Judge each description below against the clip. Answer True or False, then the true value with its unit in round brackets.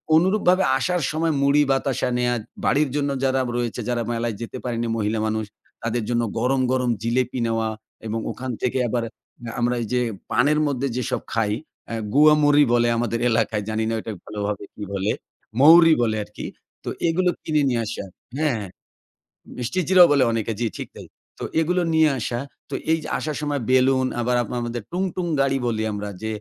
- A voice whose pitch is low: True (125 Hz)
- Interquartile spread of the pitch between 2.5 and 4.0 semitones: False (4.4 semitones)